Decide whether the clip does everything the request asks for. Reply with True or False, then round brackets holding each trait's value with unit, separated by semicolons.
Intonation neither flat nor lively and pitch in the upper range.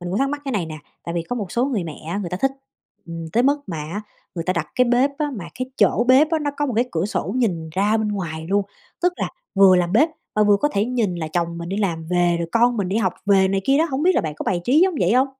False (6.5 semitones; 200 Hz)